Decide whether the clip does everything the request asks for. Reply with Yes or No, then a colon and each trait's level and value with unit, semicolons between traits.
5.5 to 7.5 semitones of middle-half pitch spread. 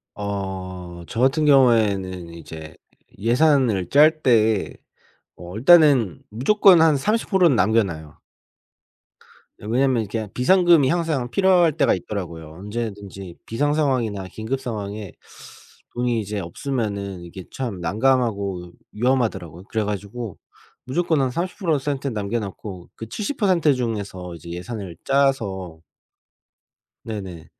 Yes: wide, 6.1 semitones